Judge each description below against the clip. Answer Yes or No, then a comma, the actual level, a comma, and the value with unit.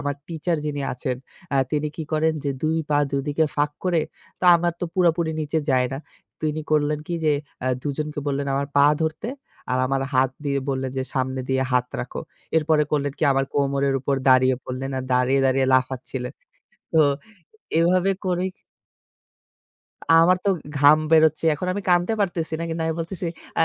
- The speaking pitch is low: No, medium, 145 Hz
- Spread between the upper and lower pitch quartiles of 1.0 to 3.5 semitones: Yes, average, 3.2 semitones